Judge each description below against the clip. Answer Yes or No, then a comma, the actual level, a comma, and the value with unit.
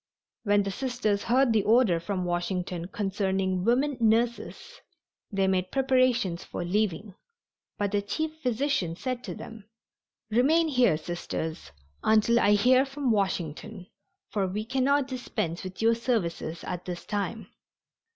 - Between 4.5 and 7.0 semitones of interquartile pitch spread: Yes, average, 5.2 semitones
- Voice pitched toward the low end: No, high, 210 Hz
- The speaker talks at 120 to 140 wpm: Yes, slow, 135 wpm